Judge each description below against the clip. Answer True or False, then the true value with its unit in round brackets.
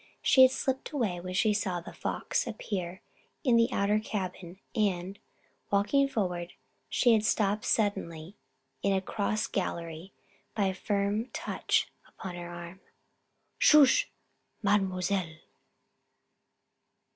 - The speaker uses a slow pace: True (120 wpm)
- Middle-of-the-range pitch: False (200 Hz)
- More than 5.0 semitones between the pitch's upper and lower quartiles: False (3.2 semitones)